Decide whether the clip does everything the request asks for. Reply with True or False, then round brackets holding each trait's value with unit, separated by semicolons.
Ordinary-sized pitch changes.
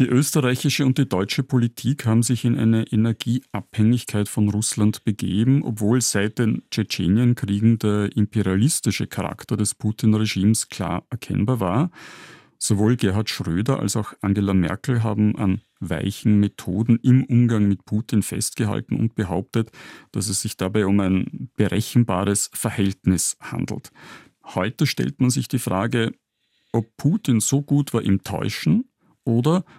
True (3.4 semitones)